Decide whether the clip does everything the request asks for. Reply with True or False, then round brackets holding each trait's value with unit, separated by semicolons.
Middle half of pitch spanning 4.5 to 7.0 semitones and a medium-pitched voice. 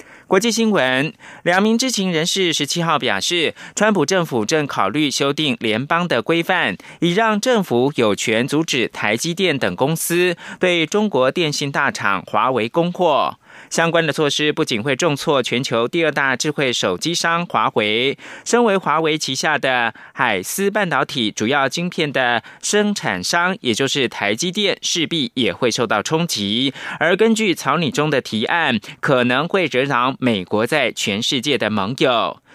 True (5.2 semitones; 160 Hz)